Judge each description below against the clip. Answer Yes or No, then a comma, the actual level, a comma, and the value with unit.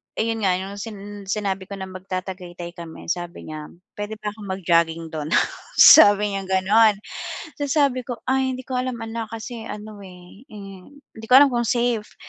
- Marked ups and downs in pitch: No, average, 3.7 semitones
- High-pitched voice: Yes, high, 205 Hz